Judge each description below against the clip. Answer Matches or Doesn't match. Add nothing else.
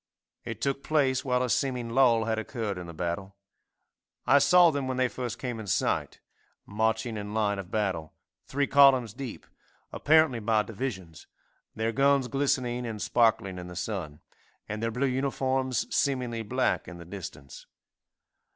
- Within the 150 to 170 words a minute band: Matches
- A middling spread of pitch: Matches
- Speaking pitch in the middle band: Doesn't match